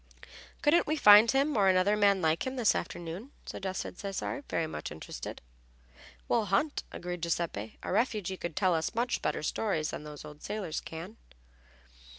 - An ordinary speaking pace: Yes, average, 160 wpm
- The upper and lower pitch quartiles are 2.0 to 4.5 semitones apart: No, average, 5.1 semitones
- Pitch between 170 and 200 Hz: Yes, high, 190 Hz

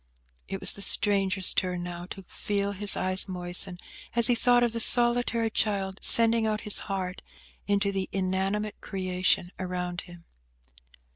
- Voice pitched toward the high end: Yes, high, 195 Hz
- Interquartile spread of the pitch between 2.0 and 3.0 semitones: Yes, narrow, 2.5 semitones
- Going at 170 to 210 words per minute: No, average, 150 wpm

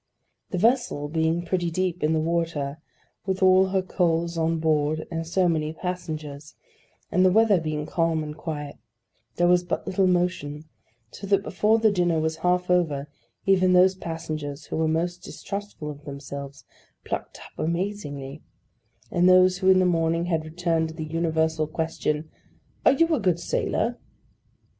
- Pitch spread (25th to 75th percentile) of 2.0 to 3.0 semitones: Yes, average, 2.7 semitones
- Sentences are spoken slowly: No, average, 160 wpm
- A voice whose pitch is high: No, medium, 165 Hz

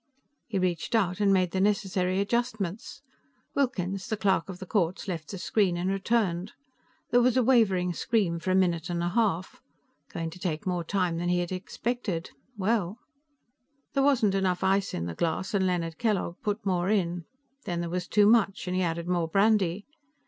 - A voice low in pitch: No, medium, 185 Hz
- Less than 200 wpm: Yes, average, 185 wpm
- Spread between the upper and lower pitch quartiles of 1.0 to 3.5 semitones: Yes, average, 3.0 semitones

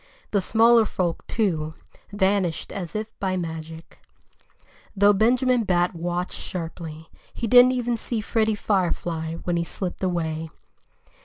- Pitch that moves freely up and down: No, average, 4.7 semitones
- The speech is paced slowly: Yes, slow, 130 wpm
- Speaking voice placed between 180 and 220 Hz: Yes, medium, 185 Hz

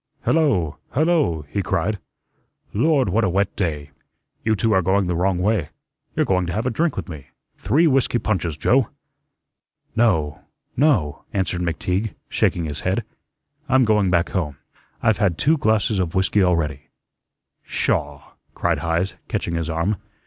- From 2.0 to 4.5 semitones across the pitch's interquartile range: No, average, 5.1 semitones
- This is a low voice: Yes, very low, 95 Hz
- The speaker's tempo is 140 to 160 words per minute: Yes, average, 155 wpm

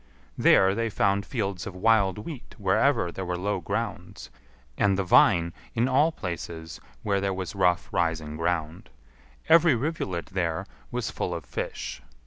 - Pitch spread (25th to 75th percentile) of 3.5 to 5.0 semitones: Yes, average, 4.2 semitones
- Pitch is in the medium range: No, very low, 95 Hz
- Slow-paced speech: No, average, 150 wpm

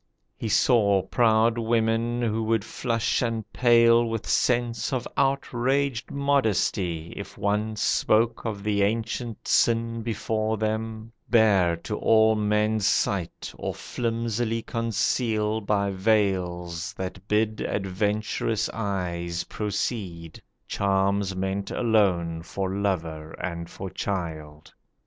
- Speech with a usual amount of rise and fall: Yes, average, 3.0 semitones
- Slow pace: Yes, slow, 110 wpm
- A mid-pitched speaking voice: No, low, 110 Hz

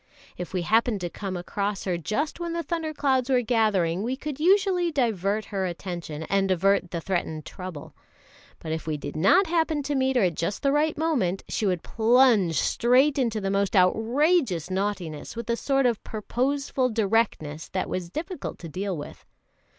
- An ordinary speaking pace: Yes, average, 180 wpm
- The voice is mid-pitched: No, high, 215 Hz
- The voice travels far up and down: Yes, wide, 6.9 semitones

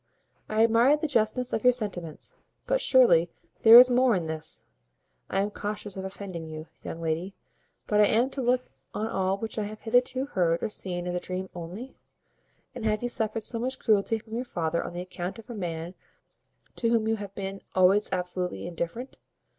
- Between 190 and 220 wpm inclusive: Yes, average, 195 wpm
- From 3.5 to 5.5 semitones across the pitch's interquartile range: Yes, average, 4.5 semitones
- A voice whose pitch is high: Yes, high, 210 Hz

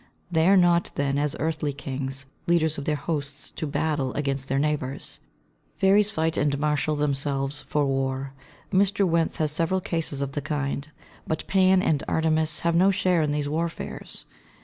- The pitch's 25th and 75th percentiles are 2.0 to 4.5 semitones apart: Yes, average, 3.0 semitones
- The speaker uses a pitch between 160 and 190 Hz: No, medium, 150 Hz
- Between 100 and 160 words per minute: No, average, 170 wpm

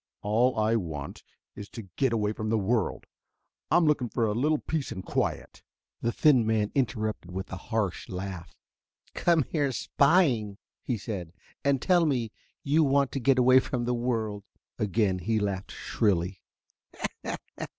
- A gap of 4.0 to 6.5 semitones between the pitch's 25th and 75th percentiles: Yes, average, 4.7 semitones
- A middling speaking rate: Yes, average, 155 wpm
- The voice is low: Yes, low, 115 Hz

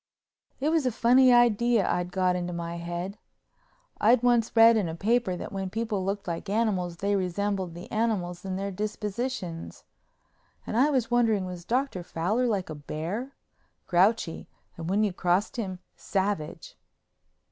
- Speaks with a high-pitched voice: Yes, high, 200 Hz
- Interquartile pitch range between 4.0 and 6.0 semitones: Yes, average, 4.5 semitones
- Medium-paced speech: Yes, average, 155 wpm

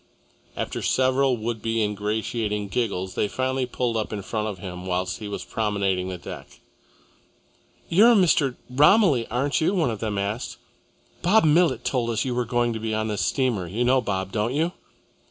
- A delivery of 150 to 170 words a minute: No, average, 185 wpm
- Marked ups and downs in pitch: No, average, 4.0 semitones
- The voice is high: No, low, 115 Hz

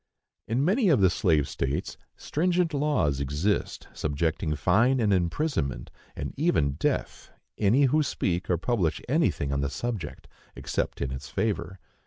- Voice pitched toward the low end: Yes, very low, 95 Hz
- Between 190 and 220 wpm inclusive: No, average, 150 wpm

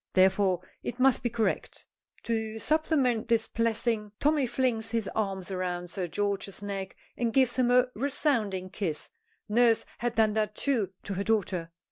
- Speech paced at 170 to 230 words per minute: No, average, 155 wpm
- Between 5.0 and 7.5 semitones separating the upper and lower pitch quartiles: No, average, 3.6 semitones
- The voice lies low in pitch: No, high, 220 Hz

